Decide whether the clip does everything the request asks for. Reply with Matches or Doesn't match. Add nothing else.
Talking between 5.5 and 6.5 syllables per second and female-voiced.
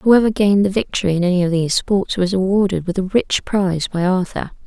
Matches